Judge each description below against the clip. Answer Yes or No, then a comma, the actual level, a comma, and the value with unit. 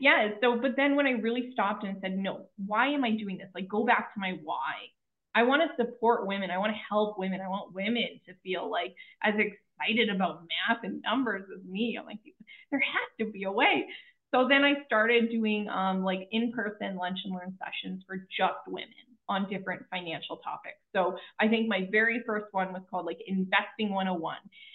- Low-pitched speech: No, high, 210 Hz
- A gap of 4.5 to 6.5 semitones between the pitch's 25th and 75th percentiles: No, average, 3.8 semitones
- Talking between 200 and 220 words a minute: Yes, fast, 205 wpm